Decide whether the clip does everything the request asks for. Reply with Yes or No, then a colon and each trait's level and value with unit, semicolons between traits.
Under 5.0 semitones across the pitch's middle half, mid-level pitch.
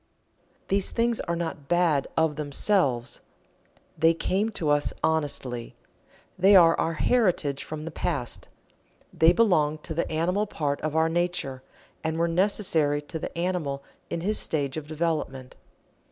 Yes: average, 3.3 semitones; medium, 160 Hz